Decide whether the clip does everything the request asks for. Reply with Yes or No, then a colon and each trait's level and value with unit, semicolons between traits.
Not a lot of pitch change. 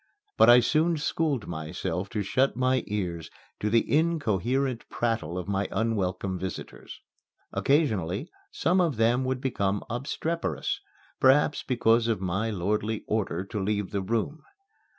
No: wide, 5.5 semitones